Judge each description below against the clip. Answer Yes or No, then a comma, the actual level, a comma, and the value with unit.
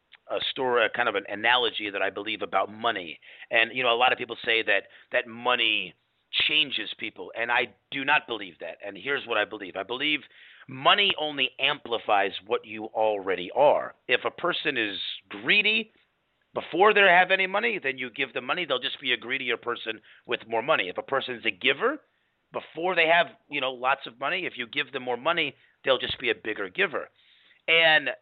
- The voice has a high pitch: No, low, 135 Hz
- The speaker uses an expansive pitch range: Yes, wide, 6.3 semitones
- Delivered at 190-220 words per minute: Yes, fast, 205 wpm